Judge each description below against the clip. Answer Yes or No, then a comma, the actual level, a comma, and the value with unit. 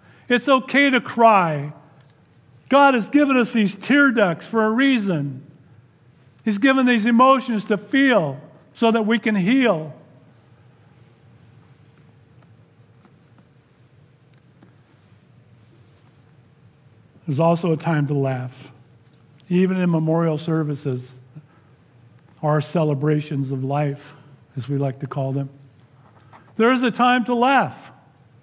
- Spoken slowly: Yes, slow, 110 wpm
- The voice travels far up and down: Yes, wide, 8.1 semitones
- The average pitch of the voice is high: No, medium, 145 Hz